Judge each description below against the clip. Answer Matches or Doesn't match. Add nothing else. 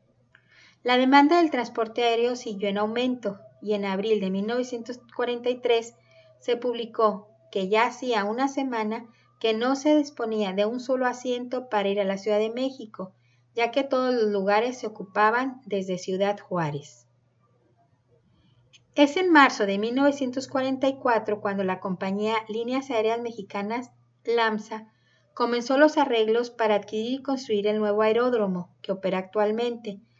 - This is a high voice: Matches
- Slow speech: Doesn't match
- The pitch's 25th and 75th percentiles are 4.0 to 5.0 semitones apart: Doesn't match